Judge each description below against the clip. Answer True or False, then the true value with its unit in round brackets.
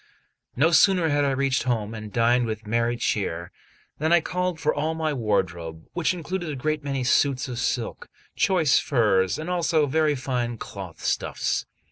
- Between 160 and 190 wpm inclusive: True (170 wpm)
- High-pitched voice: False (135 Hz)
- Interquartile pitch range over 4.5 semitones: True (5.6 semitones)